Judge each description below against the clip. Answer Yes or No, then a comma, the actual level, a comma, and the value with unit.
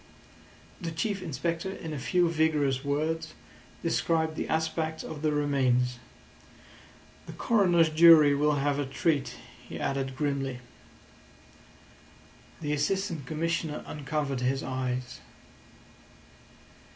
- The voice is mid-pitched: Yes, medium, 150 Hz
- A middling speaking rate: No, slow, 105 wpm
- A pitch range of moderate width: Yes, average, 3.0 semitones